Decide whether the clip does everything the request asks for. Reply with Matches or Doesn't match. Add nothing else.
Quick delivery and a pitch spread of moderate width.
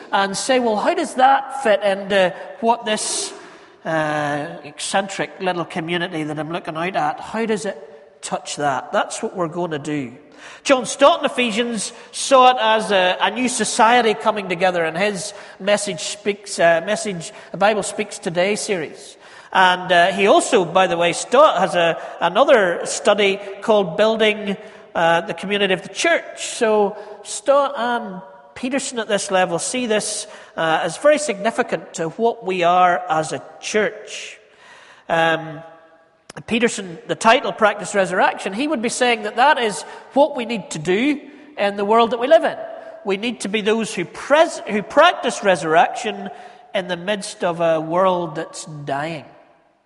Doesn't match